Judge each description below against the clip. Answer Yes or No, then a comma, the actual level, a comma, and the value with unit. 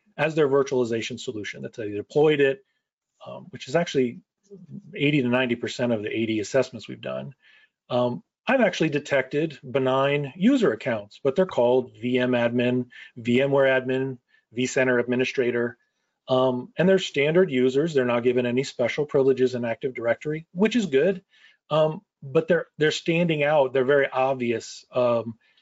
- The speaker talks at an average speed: Yes, average, 150 wpm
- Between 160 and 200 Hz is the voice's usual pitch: No, low, 135 Hz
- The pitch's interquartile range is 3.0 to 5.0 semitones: Yes, average, 3.9 semitones